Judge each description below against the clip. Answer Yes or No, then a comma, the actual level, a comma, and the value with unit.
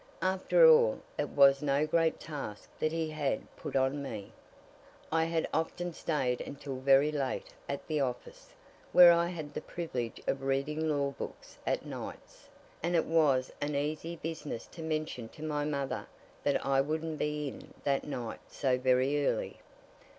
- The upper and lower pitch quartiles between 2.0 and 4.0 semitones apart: Yes, average, 2.9 semitones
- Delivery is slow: No, average, 165 wpm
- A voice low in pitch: No, medium, 150 Hz